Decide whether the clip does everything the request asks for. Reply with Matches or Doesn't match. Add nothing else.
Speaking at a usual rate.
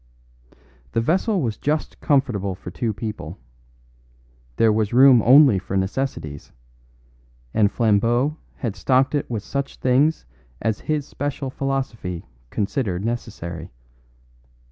Doesn't match